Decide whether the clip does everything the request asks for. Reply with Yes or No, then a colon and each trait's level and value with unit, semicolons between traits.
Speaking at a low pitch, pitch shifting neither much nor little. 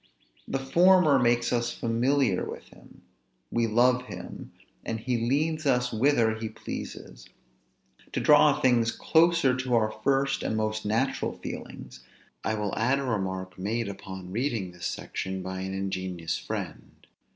Yes: low, 115 Hz; average, 4.9 semitones